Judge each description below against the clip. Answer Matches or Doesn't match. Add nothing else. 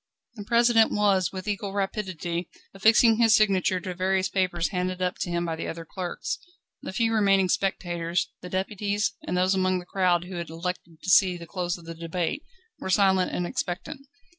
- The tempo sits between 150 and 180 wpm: Doesn't match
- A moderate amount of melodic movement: Doesn't match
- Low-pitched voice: Doesn't match